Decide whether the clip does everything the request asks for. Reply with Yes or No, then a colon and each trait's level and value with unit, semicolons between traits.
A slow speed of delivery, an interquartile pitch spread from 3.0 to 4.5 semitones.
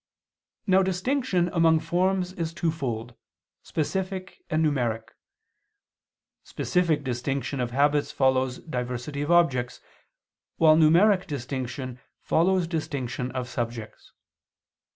No: slow, 95 wpm; wide, 5.4 semitones